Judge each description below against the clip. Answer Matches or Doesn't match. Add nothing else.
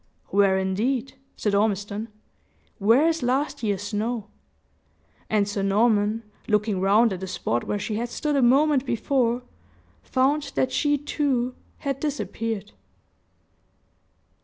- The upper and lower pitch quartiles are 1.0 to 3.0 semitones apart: Doesn't match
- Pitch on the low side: Doesn't match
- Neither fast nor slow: Doesn't match